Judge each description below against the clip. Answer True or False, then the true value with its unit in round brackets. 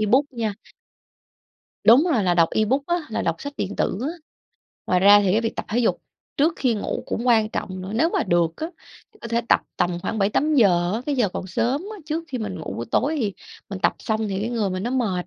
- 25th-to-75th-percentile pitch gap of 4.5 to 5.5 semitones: True (5.2 semitones)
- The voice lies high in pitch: True (220 Hz)